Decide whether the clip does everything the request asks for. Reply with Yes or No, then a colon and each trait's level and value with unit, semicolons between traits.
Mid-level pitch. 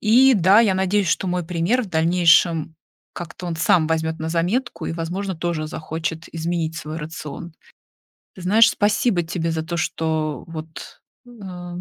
Yes: medium, 170 Hz